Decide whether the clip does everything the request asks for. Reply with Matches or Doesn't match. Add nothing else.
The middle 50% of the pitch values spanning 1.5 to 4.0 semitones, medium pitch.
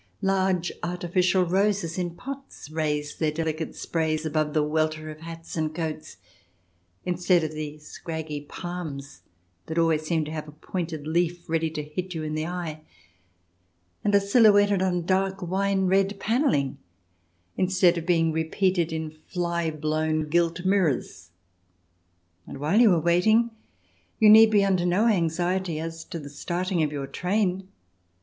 Matches